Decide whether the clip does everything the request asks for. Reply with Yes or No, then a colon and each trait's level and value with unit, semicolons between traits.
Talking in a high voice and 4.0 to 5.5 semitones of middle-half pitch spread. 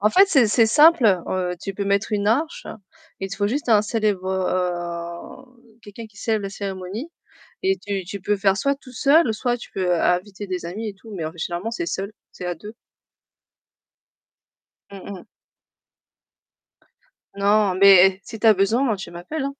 No: high, 205 Hz; average, 3.5 semitones